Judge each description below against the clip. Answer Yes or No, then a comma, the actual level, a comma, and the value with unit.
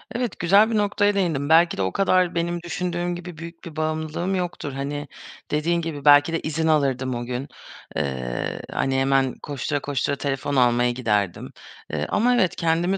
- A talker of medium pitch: Yes, medium, 155 Hz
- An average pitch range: Yes, average, 4.4 semitones